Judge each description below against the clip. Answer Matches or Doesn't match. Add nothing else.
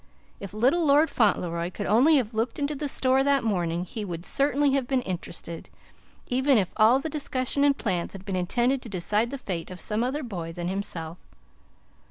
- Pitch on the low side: Doesn't match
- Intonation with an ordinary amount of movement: Doesn't match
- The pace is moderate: Matches